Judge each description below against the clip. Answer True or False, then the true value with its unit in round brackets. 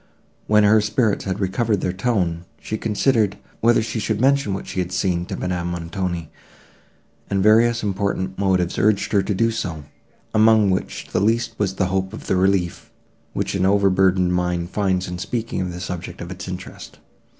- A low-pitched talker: True (95 Hz)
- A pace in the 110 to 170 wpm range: False (185 wpm)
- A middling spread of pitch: True (3.0 semitones)